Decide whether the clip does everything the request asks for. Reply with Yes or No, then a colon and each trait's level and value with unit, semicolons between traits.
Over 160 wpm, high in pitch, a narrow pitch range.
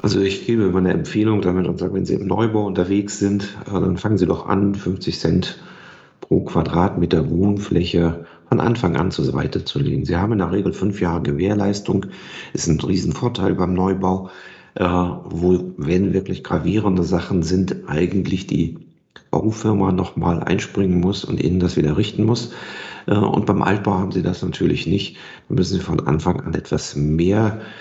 No: average, 170 wpm; very low, 95 Hz; narrow, 2.2 semitones